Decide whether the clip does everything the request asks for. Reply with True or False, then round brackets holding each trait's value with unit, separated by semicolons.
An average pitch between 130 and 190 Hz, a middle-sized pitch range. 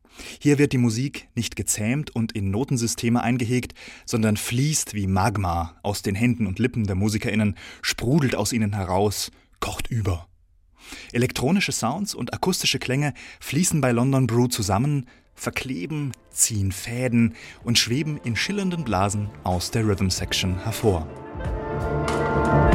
False (115 Hz; 4.4 semitones)